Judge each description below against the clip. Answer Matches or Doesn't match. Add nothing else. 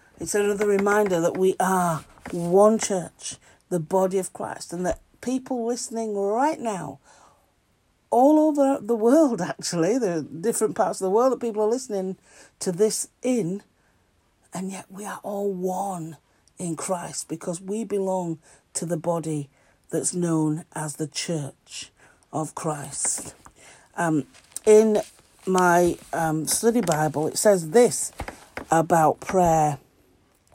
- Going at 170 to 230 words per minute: Doesn't match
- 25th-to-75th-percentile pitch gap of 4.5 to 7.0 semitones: Matches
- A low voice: Doesn't match